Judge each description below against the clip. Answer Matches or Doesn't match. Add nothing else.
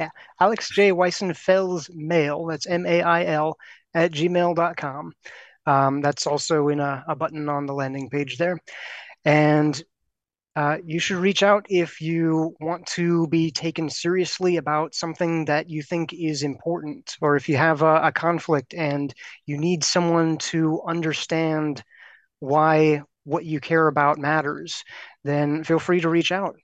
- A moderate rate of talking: Matches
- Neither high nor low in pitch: Matches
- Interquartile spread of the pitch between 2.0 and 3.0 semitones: Matches